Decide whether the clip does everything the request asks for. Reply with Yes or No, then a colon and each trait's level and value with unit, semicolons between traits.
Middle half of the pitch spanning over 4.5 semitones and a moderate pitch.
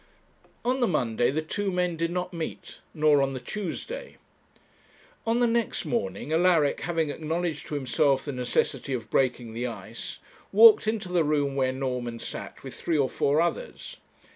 Yes: average, 5.2 semitones; medium, 155 Hz